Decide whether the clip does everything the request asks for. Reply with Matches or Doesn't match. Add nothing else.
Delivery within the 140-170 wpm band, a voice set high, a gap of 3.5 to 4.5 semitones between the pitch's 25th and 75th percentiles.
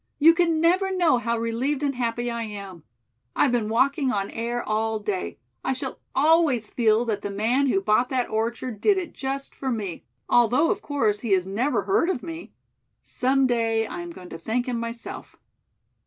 Doesn't match